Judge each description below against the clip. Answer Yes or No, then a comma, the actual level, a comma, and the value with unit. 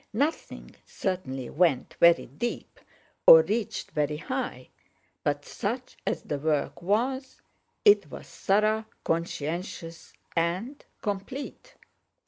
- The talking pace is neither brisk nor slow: No, slow, 100 wpm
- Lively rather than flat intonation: Yes, wide, 7.1 semitones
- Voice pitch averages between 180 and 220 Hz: Yes, high, 190 Hz